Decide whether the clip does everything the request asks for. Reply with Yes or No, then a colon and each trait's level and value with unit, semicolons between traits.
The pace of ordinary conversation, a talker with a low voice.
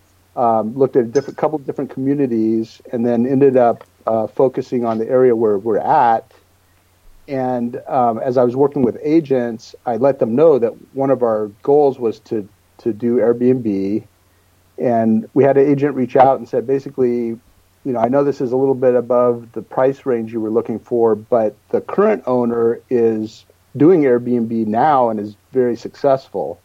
Yes: average, 185 wpm; low, 120 Hz